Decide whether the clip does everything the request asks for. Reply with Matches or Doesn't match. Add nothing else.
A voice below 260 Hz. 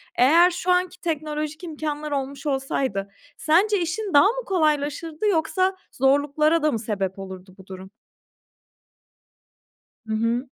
Doesn't match